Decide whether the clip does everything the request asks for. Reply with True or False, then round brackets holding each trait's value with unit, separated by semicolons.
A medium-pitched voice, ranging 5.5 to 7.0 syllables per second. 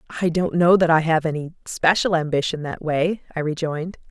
True (165 Hz; 5.7 syllables/s)